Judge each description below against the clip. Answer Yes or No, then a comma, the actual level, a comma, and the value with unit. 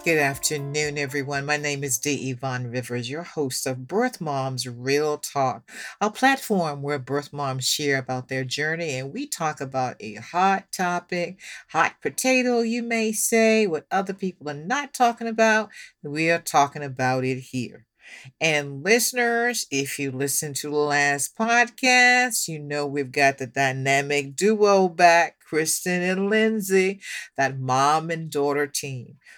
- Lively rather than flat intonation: Yes, wide, 6.2 semitones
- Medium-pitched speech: Yes, medium, 150 Hz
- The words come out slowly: No, average, 155 wpm